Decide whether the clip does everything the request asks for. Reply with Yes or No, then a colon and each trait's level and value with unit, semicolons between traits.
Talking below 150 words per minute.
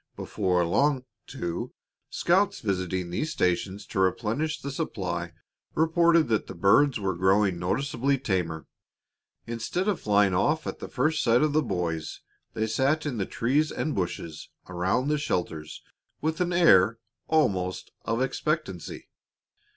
Yes: average, 140 wpm